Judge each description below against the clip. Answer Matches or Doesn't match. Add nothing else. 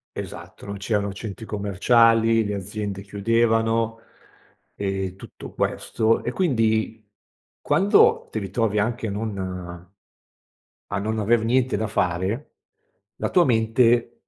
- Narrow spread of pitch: Matches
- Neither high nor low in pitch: Doesn't match